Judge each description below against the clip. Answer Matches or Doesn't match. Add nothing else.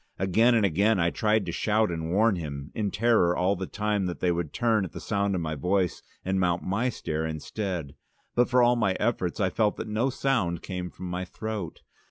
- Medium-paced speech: Doesn't match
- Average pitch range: Matches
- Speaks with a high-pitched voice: Doesn't match